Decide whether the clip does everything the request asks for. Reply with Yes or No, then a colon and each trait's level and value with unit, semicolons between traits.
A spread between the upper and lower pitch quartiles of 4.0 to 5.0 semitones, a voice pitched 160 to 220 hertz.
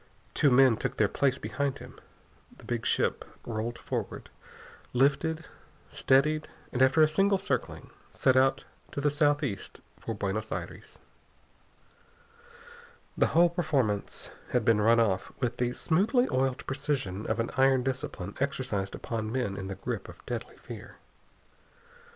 No: average, 4.5 semitones; low, 130 Hz